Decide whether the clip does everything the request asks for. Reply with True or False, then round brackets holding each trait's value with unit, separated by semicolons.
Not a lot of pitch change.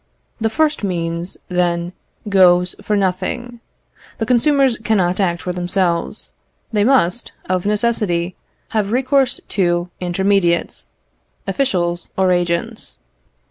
False (4.1 semitones)